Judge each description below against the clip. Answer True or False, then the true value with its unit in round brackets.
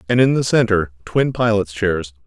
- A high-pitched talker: False (105 Hz)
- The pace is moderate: True (185 wpm)